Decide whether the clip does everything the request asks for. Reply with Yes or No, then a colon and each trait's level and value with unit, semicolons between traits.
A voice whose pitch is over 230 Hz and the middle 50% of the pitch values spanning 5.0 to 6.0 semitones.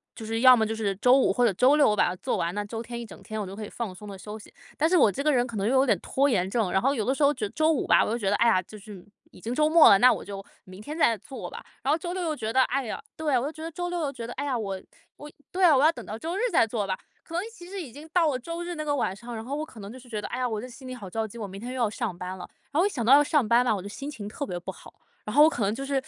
Yes: high, 245 Hz; wide, 5.6 semitones